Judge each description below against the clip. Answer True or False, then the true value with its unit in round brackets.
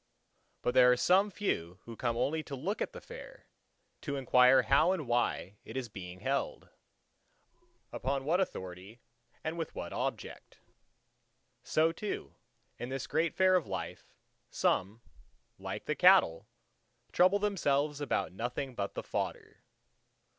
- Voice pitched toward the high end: False (135 Hz)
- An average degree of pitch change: False (5.9 semitones)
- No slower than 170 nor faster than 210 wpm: False (140 wpm)